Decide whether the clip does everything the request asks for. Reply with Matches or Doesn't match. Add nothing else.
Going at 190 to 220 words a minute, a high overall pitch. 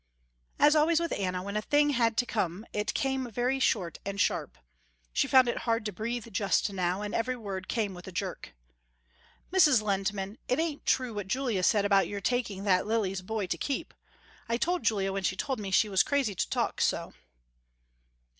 Matches